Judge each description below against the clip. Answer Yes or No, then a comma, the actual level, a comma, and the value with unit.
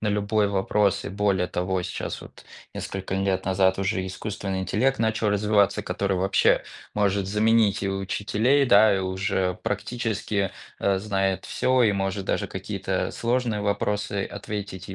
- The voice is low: Yes, low, 100 Hz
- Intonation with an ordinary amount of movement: No, narrow, 1.7 semitones